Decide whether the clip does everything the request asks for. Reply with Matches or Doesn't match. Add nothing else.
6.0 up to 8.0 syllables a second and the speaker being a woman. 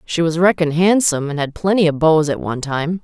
Matches